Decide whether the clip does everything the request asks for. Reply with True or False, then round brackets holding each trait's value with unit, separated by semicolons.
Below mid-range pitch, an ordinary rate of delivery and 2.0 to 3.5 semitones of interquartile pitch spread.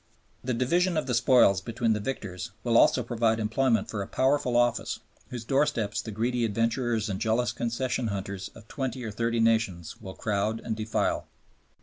True (115 Hz; 175 wpm; 2.6 semitones)